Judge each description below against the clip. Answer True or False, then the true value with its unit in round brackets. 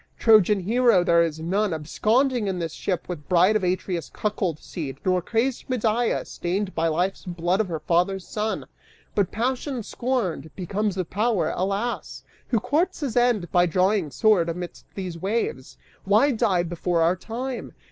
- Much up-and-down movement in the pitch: False (4.4 semitones)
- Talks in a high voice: True (195 Hz)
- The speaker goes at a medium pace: True (160 wpm)